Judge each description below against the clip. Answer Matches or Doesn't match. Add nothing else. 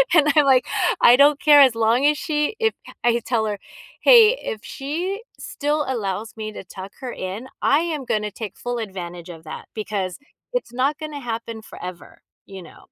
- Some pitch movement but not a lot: Doesn't match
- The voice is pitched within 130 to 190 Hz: Doesn't match